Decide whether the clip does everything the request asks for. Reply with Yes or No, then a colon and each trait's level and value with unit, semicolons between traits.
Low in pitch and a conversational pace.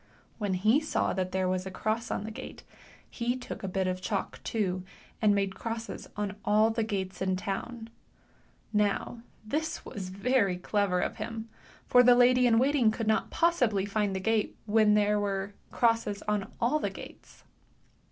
No: high, 210 Hz; average, 180 wpm